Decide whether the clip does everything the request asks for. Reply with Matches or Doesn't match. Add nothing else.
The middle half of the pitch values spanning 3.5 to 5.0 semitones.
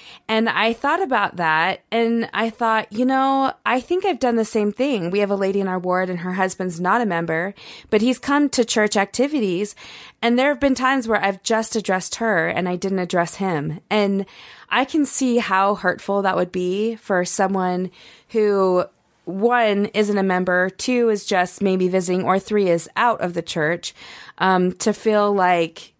Matches